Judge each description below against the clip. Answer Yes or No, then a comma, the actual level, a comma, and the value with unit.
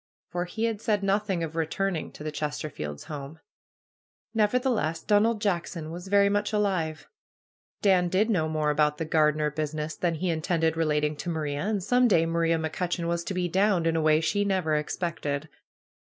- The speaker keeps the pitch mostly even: No, average, 4.2 semitones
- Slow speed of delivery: No, average, 180 wpm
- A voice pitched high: No, medium, 165 Hz